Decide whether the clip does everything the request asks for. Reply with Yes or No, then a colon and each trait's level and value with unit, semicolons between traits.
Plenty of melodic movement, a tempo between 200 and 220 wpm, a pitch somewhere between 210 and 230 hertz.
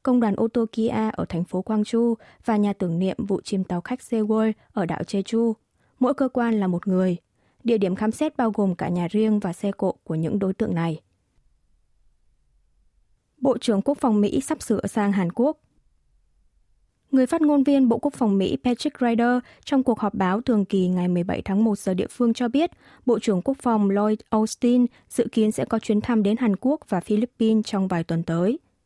No: average, 4.2 semitones; average, 205 wpm; high, 215 Hz